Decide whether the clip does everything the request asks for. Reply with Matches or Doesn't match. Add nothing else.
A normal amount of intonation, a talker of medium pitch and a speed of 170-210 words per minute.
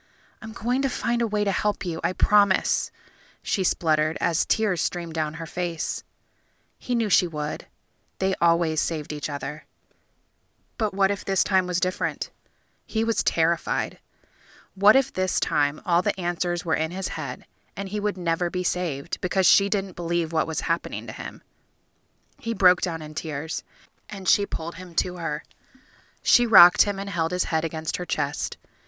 Matches